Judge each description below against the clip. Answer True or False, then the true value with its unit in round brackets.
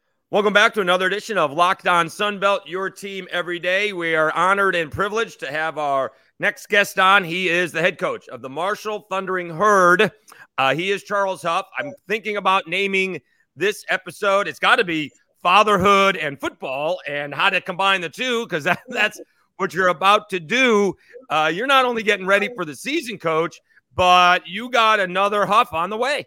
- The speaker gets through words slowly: False (190 wpm)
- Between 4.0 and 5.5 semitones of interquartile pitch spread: False (2.9 semitones)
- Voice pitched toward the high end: True (195 Hz)